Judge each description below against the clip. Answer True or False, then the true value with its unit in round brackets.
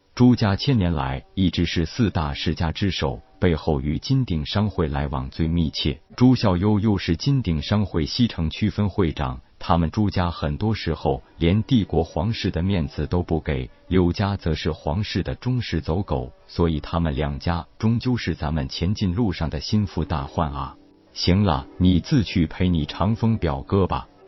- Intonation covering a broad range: False (4.8 semitones)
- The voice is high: False (85 Hz)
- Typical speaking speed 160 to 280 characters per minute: True (255 characters per minute)